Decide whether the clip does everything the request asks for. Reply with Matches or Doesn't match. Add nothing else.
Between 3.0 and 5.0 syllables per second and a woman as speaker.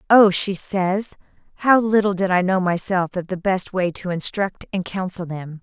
Matches